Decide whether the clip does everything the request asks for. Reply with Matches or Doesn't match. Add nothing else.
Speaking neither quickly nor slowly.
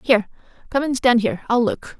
Doesn't match